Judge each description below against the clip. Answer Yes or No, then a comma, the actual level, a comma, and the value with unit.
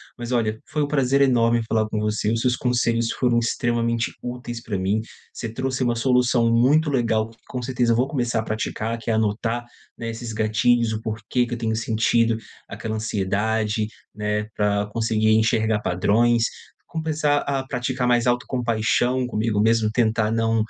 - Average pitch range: No, narrow, 2.0 semitones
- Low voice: Yes, low, 115 Hz